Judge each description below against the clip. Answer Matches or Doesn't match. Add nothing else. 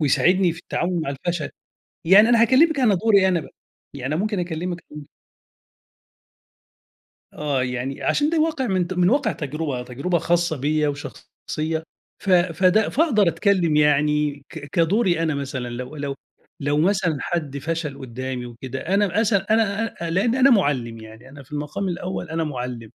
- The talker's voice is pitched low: Doesn't match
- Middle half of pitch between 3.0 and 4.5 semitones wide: Doesn't match